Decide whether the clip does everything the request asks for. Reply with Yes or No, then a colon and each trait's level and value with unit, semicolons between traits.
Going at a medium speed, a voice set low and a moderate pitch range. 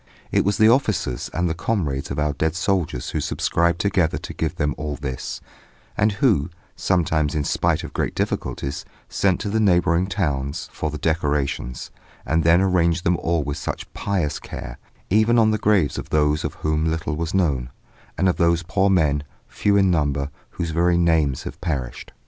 Yes: average, 185 wpm; very low, 80 Hz; average, 4.1 semitones